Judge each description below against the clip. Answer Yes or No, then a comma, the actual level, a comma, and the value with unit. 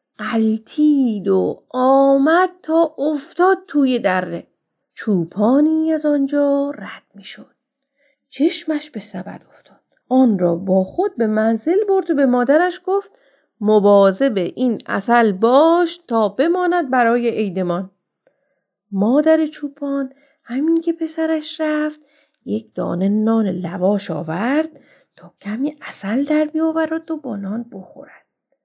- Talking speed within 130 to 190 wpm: No, average, 120 wpm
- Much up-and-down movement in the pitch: Yes, wide, 6.4 semitones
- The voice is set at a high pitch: Yes, very high, 270 Hz